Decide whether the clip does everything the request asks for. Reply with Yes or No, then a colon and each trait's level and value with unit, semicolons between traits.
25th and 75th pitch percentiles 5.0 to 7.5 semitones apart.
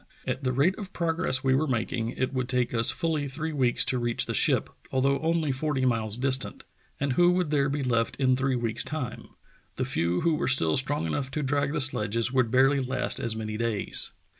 No: average, 3.4 semitones